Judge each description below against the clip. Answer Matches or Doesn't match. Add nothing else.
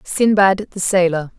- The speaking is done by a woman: Matches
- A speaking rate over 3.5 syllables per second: Matches